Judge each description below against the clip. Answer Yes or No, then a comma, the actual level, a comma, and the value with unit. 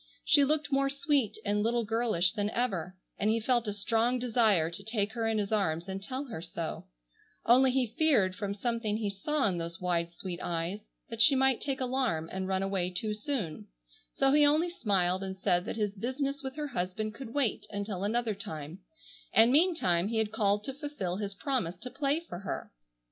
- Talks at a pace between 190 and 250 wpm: Yes, average, 200 wpm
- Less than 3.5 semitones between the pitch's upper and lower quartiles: No, wide, 5.6 semitones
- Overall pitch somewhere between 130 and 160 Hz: No, high, 215 Hz